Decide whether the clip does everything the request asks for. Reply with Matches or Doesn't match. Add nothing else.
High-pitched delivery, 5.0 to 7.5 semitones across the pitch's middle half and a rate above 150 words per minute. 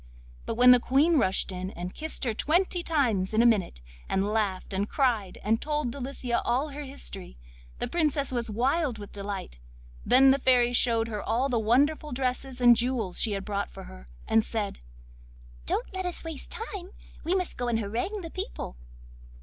Matches